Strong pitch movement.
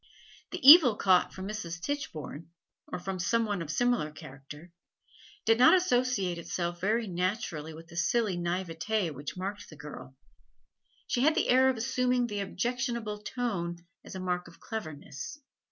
Yes: wide, 5.9 semitones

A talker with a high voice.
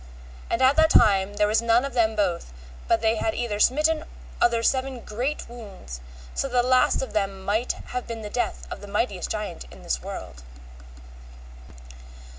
Yes: high, 230 Hz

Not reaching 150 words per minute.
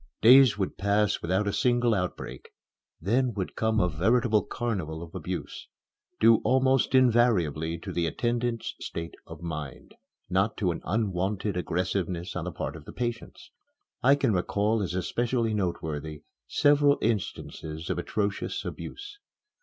Yes: average, 140 wpm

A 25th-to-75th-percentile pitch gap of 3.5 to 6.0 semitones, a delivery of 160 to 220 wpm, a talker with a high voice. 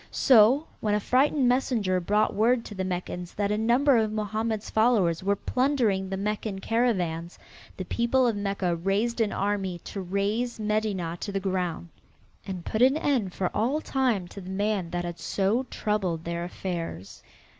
Yes: average, 3.8 semitones; average, 170 wpm; high, 205 Hz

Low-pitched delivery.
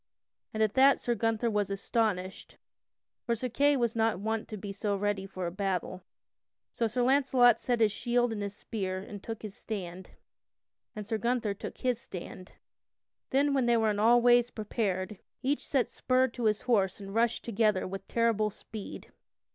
No: high, 220 Hz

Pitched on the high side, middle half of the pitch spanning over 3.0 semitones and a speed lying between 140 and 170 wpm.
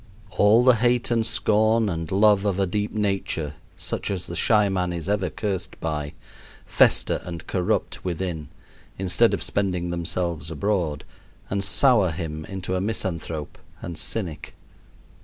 No: very low, 95 Hz; average, 3.7 semitones; average, 145 wpm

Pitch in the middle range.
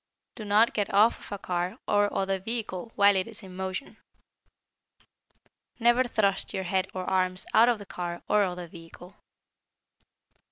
No: high, 195 Hz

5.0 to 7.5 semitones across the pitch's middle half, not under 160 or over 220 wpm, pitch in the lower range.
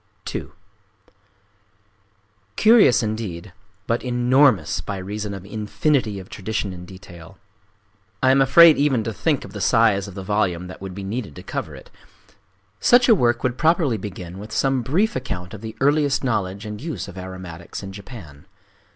Yes: wide, 5.5 semitones; average, 170 wpm; low, 110 Hz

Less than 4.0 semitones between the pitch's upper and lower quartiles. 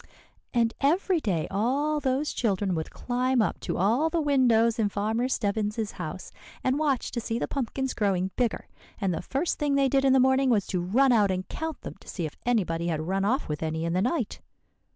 No: wide, 5.5 semitones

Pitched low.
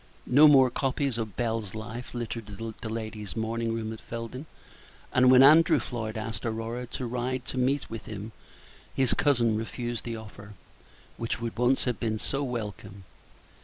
Yes: low, 115 Hz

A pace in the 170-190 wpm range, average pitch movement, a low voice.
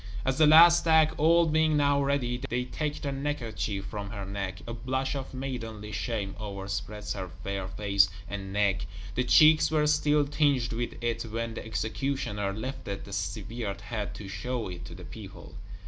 No: average, 175 wpm; wide, 6.0 semitones; low, 115 Hz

